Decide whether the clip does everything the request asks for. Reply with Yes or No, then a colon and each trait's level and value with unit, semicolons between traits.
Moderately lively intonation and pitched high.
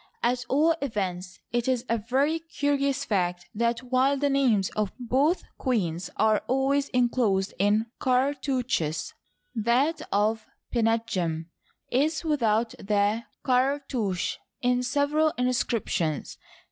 Yes: average, 4.6 semitones; high, 245 Hz